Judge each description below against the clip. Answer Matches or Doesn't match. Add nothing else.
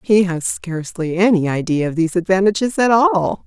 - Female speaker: Matches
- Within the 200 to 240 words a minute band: Doesn't match